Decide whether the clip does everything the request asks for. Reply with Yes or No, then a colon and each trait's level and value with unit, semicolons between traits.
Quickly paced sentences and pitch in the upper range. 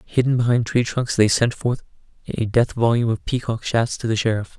No: fast, 210 wpm; low, 115 Hz